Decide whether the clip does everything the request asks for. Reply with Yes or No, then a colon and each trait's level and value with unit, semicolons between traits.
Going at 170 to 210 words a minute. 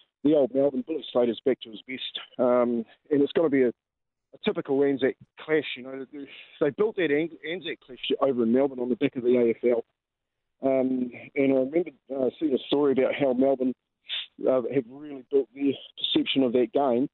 Yes: fast, 205 wpm